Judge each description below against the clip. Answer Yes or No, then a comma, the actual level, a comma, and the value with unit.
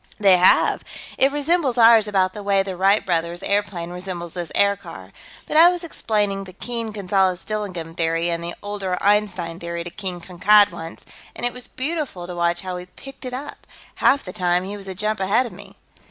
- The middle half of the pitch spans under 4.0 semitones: Yes, average, 3.3 semitones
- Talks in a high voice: Yes, high, 195 Hz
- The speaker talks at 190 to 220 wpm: Yes, average, 200 wpm